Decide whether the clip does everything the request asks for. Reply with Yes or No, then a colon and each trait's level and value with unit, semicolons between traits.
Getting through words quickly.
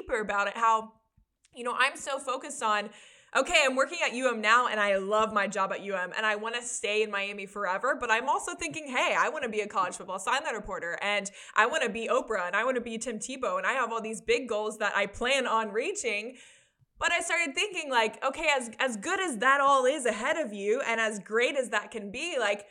Yes: fast, 250 wpm